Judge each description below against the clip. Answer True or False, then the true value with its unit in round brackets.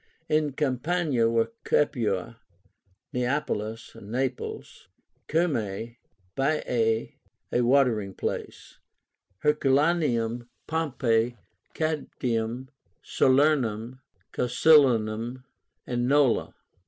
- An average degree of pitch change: True (4.3 semitones)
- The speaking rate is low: True (65 wpm)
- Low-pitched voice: True (125 Hz)